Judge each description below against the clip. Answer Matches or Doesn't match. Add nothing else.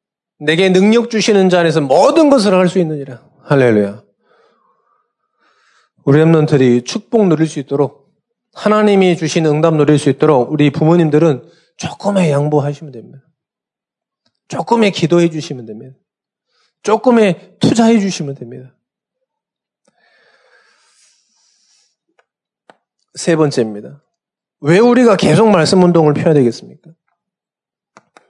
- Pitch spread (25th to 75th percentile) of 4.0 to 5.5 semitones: Doesn't match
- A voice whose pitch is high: Doesn't match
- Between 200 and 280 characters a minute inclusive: Matches